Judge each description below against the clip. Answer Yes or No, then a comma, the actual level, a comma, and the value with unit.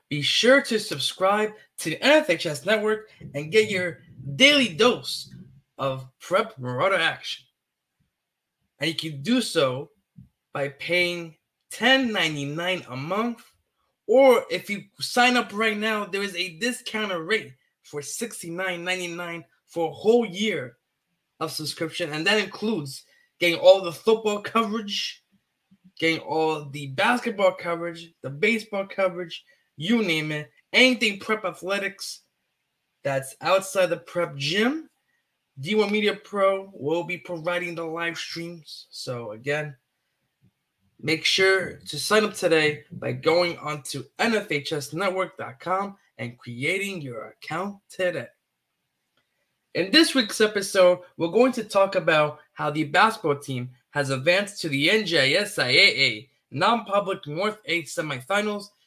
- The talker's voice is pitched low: No, medium, 180 Hz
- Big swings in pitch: Yes, wide, 5.8 semitones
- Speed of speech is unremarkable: No, slow, 125 wpm